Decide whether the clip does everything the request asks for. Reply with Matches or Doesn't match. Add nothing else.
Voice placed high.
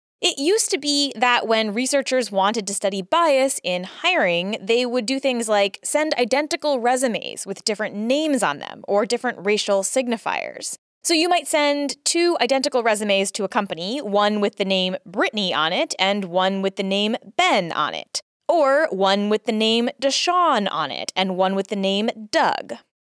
Matches